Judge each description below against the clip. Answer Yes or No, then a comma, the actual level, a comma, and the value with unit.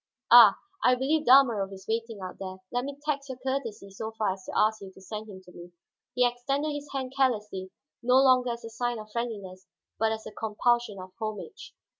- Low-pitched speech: No, high, 230 Hz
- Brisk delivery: Yes, fast, 210 wpm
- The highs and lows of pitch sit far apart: No, average, 4.1 semitones